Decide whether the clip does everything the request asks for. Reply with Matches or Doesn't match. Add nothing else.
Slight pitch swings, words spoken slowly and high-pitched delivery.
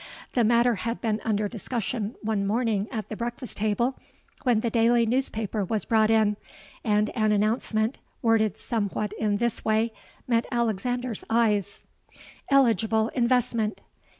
Matches